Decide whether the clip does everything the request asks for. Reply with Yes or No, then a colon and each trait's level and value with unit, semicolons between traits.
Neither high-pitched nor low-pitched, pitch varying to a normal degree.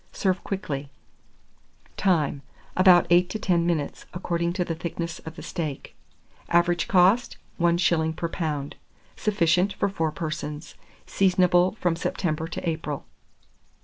No: medium, 170 Hz; narrow, 2.2 semitones